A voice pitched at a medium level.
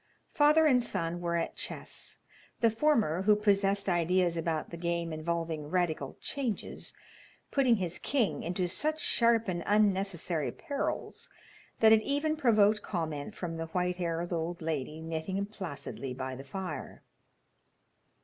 Yes: medium, 180 Hz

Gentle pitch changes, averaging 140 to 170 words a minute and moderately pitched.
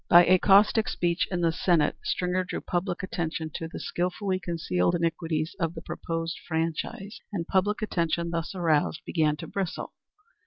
Yes: narrow, 2.2 semitones; average, 160 wpm; medium, 170 Hz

